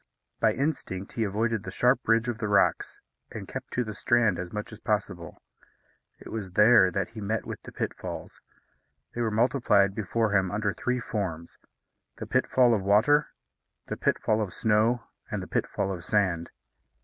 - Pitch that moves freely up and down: No, average, 3.1 semitones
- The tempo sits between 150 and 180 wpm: Yes, average, 175 wpm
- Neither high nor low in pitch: No, low, 105 Hz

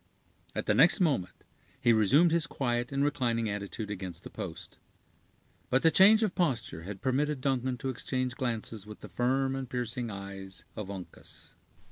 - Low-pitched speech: Yes, low, 125 Hz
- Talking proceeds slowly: No, average, 165 wpm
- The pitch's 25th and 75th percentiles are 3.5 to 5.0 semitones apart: Yes, average, 4.5 semitones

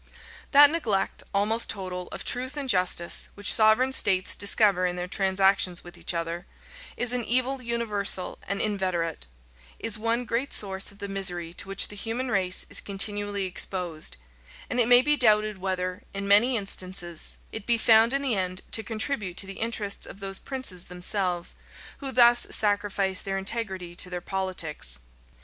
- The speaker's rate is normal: Yes, average, 170 wpm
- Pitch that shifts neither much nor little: Yes, average, 3.8 semitones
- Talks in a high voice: Yes, high, 200 Hz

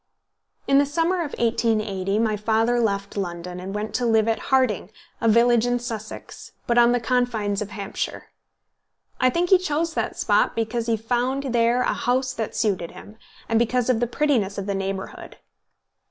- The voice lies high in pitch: Yes, high, 230 Hz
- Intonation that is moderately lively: Yes, average, 3.1 semitones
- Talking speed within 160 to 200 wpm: Yes, average, 180 wpm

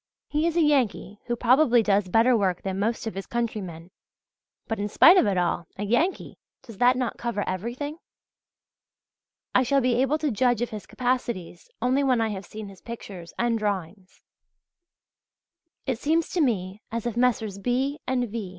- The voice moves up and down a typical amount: Yes, average, 4.2 semitones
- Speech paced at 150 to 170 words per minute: No, average, 180 wpm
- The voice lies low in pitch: No, high, 230 Hz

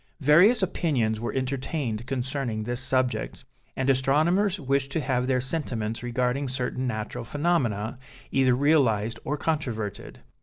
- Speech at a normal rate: No, slow, 125 wpm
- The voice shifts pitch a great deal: No, average, 3.2 semitones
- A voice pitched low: Yes, low, 130 Hz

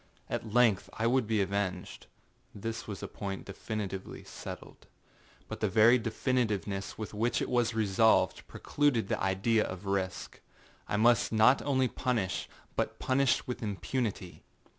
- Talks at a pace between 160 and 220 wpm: No, average, 140 wpm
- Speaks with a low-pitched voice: Yes, low, 110 Hz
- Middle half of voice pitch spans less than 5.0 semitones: Yes, average, 3.6 semitones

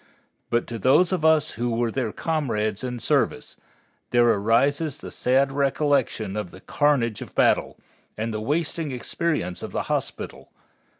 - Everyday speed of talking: Yes, average, 155 wpm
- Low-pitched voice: Yes, low, 125 Hz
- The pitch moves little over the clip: No, average, 4.8 semitones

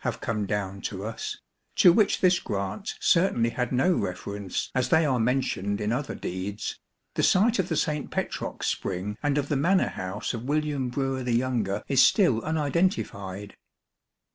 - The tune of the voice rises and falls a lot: Yes, wide, 6.7 semitones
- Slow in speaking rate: No, average, 165 wpm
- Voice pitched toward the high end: No, low, 125 Hz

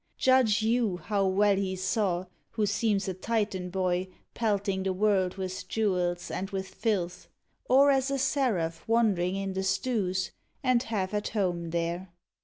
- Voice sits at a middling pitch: No, high, 195 Hz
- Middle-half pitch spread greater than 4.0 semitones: No, average, 3.2 semitones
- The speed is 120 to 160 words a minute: Yes, average, 155 wpm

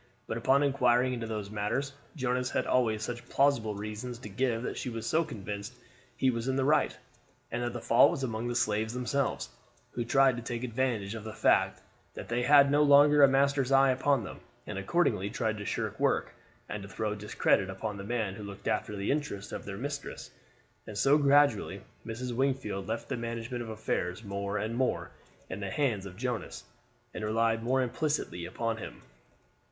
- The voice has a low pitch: Yes, low, 115 Hz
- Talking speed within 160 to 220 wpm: Yes, average, 190 wpm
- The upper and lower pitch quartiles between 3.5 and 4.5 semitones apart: Yes, average, 3.8 semitones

